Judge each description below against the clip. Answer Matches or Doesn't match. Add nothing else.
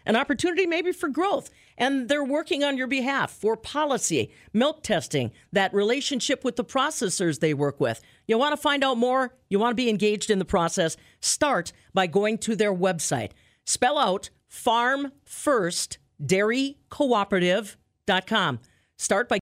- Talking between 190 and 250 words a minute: Doesn't match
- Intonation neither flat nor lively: Doesn't match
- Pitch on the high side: Matches